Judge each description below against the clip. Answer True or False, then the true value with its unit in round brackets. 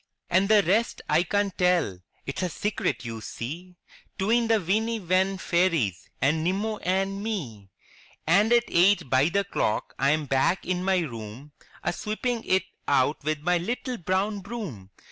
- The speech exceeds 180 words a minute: False (165 wpm)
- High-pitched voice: False (180 Hz)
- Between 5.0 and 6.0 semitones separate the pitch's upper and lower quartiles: True (5.3 semitones)